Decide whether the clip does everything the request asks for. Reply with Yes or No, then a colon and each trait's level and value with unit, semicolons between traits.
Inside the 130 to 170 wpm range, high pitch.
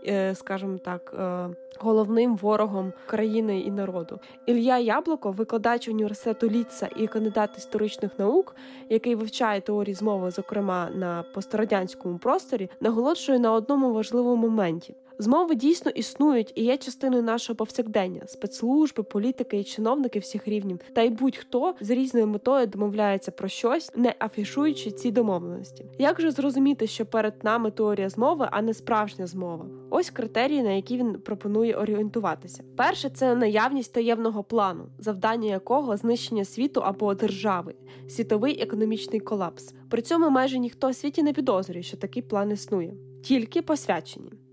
Yes: average, 140 wpm; high, 220 Hz